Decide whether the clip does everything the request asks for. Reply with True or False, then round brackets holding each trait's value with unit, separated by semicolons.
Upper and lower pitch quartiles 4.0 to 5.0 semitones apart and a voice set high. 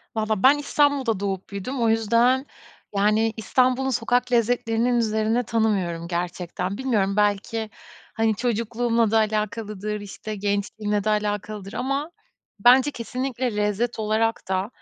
False (2.8 semitones; 220 Hz)